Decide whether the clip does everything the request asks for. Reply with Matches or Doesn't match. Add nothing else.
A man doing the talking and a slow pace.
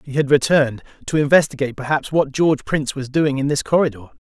Doesn't match